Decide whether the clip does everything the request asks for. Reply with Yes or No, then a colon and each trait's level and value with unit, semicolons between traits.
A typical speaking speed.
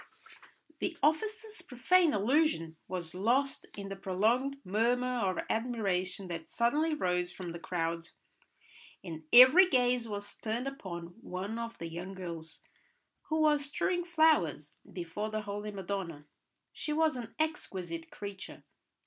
No: slow, 130 wpm